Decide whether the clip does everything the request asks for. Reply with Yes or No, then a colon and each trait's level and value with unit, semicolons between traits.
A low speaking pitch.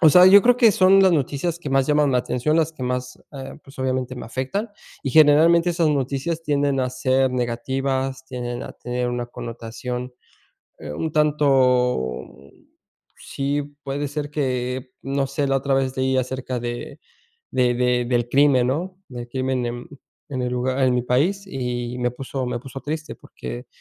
Yes: low, 130 Hz